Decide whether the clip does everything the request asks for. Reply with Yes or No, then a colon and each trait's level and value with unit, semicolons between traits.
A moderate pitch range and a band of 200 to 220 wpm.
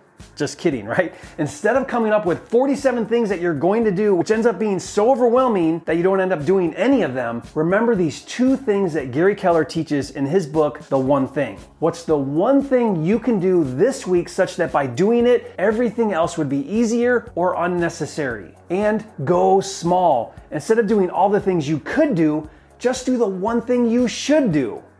No: wide, 6.4 semitones; fast, 205 wpm